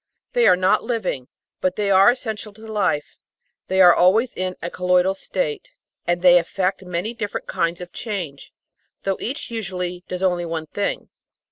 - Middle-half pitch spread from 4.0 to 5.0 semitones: No, average, 3.3 semitones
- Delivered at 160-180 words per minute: Yes, average, 170 wpm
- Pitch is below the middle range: No, medium, 185 Hz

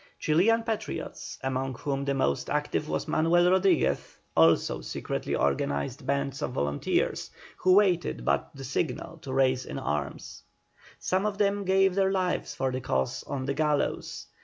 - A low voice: No, medium, 145 Hz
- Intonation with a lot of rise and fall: Yes, wide, 6.1 semitones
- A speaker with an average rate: Yes, average, 155 wpm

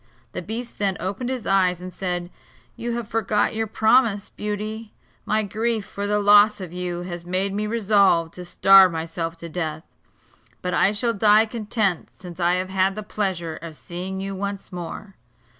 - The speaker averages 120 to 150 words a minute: No, average, 175 wpm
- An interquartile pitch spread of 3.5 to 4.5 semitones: No, average, 3.0 semitones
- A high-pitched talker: Yes, high, 195 Hz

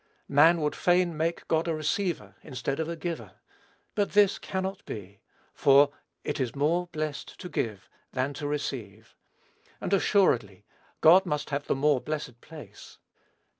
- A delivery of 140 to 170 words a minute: Yes, average, 150 wpm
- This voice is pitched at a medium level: Yes, medium, 150 Hz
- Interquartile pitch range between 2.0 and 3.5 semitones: No, average, 4.4 semitones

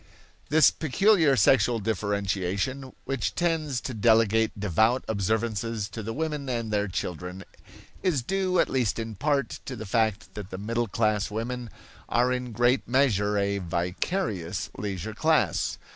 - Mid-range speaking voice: No, low, 115 Hz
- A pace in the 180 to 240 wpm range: No, average, 145 wpm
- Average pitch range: Yes, average, 4.3 semitones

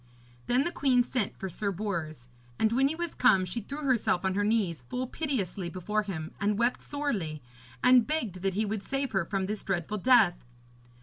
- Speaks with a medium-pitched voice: No, high, 210 Hz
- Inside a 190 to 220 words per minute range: Yes, average, 195 wpm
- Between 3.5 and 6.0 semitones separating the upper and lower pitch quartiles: Yes, average, 5.2 semitones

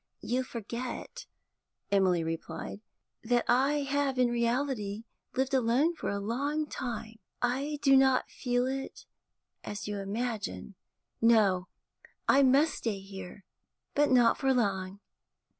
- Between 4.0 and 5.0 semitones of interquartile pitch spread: Yes, average, 4.6 semitones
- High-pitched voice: Yes, high, 240 Hz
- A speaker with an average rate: No, slow, 125 wpm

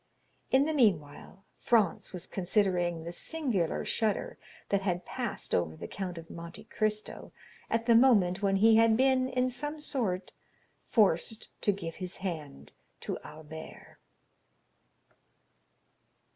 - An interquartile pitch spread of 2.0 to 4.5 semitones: No, average, 5.2 semitones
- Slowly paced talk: Yes, slow, 130 wpm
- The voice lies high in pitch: Yes, high, 195 Hz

